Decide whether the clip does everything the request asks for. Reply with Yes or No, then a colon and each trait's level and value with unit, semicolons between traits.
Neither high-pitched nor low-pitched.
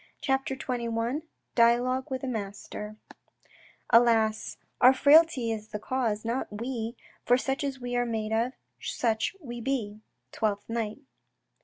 No: high, 235 Hz